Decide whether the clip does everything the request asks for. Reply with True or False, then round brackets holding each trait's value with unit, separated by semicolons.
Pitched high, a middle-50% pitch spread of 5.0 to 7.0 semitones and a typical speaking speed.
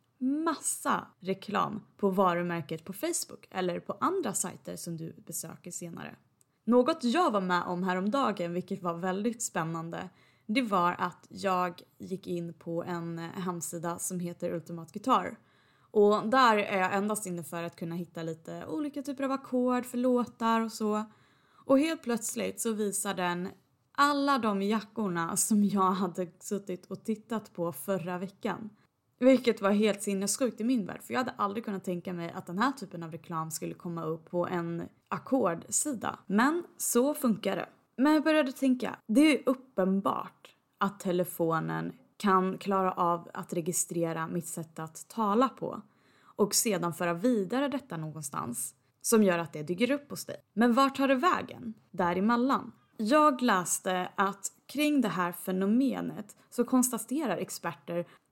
True (195 Hz; 5.5 semitones; 155 wpm)